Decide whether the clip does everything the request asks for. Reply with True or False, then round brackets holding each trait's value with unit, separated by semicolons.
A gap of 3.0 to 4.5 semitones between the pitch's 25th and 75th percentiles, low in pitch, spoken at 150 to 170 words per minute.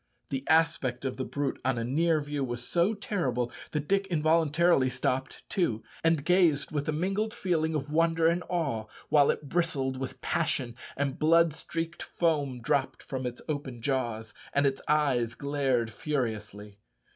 False (4.1 semitones; 145 Hz; 160 wpm)